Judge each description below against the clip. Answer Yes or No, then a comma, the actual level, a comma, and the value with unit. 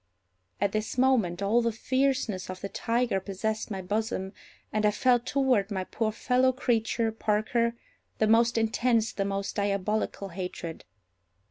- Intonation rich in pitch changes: No, average, 3.0 semitones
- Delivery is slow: No, average, 145 wpm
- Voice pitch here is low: No, high, 220 Hz